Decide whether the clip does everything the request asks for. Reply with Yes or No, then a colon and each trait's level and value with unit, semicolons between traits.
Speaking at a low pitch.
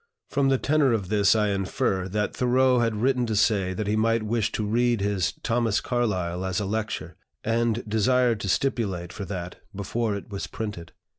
Yes: low, 110 Hz